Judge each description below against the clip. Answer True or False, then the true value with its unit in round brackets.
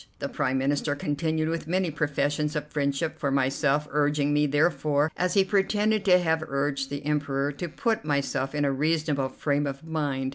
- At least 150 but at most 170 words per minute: False (180 wpm)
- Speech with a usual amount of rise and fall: False (2.3 semitones)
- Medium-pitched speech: True (150 Hz)